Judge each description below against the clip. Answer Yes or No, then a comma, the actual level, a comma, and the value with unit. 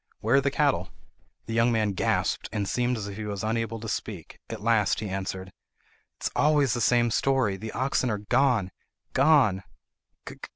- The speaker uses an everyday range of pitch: Yes, average, 3.8 semitones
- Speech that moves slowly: No, average, 170 wpm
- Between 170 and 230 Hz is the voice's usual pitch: No, low, 115 Hz